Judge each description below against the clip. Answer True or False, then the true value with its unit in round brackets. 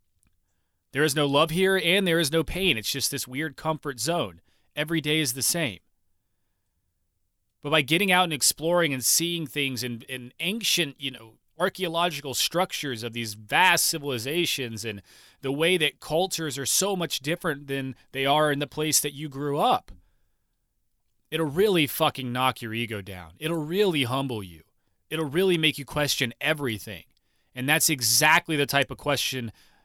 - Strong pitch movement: True (5.9 semitones)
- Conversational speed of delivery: True (170 wpm)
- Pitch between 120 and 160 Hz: True (140 Hz)